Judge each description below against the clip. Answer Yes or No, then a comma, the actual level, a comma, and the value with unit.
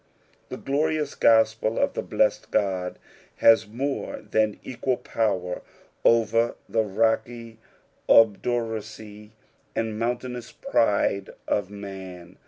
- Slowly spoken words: Yes, slow, 100 wpm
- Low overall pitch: Yes, low, 110 Hz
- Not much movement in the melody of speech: Yes, narrow, 2.3 semitones